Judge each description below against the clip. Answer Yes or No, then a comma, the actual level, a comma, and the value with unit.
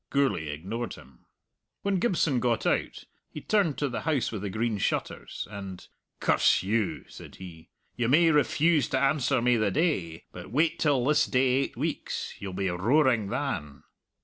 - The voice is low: Yes, low, 120 Hz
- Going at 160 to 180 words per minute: Yes, average, 170 wpm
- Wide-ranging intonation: Yes, wide, 7.1 semitones